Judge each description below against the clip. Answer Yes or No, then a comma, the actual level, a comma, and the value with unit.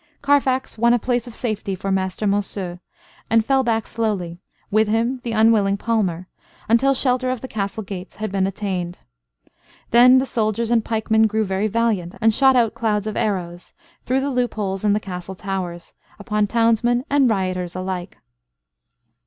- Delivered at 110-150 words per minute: No, average, 165 wpm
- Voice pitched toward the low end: No, high, 215 Hz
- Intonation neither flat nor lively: Yes, average, 3.6 semitones